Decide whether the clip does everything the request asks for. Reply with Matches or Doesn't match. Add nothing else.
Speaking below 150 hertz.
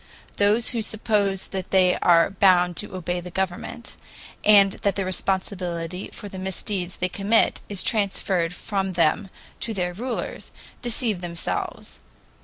Doesn't match